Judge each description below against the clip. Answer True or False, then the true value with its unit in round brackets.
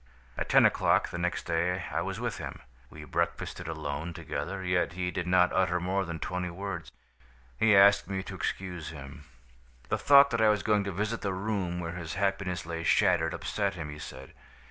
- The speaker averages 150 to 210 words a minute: True (195 wpm)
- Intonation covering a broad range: False (2.8 semitones)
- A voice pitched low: True (90 Hz)